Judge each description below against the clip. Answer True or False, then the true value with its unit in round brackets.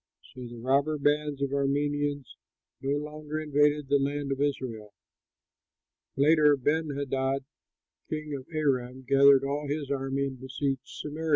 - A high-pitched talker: False (140 Hz)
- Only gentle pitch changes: True (1.6 semitones)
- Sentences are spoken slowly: True (130 wpm)